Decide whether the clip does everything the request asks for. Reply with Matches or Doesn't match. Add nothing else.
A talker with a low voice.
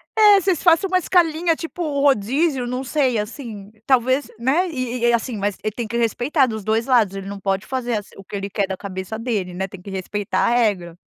Doesn't match